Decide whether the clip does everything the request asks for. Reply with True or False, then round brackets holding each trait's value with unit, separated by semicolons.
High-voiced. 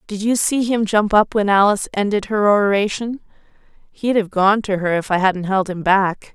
True (205 Hz)